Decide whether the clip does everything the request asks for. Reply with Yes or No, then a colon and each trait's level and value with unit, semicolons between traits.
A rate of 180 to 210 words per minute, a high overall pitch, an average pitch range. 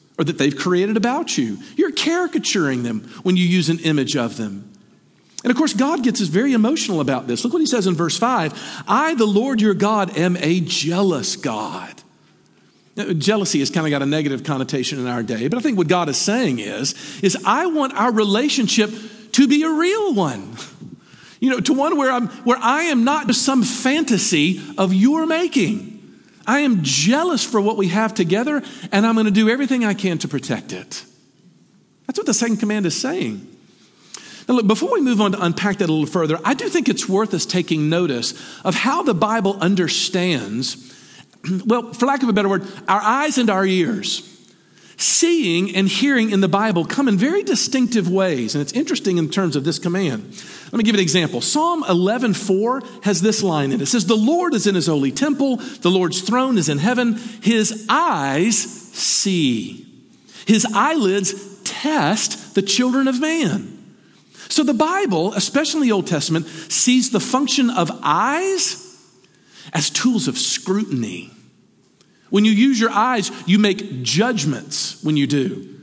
No: average, 185 wpm; high, 210 Hz; wide, 6.0 semitones